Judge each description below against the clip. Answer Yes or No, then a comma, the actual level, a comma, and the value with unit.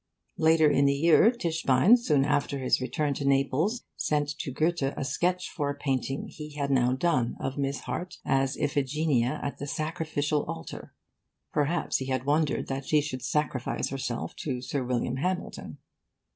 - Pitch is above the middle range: No, medium, 145 Hz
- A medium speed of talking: Yes, average, 165 wpm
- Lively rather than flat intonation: No, average, 2.8 semitones